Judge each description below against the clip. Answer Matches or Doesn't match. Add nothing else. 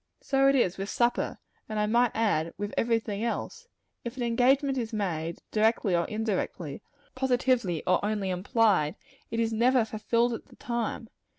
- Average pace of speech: Matches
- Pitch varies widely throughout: Doesn't match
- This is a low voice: Doesn't match